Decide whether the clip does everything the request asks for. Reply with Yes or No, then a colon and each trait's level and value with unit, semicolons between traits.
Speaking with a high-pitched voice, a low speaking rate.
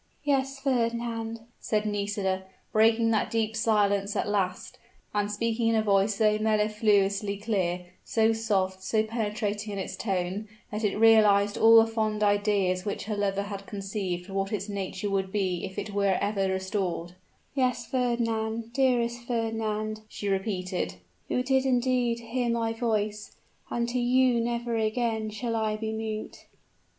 No: high, 215 Hz; average, 155 wpm